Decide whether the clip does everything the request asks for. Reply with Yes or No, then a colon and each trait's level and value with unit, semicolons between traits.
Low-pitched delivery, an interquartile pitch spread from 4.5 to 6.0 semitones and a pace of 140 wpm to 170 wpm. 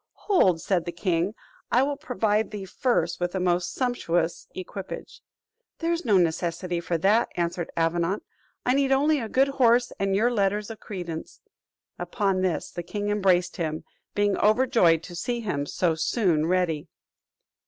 No: high, 195 Hz; average, 5.3 semitones; average, 160 wpm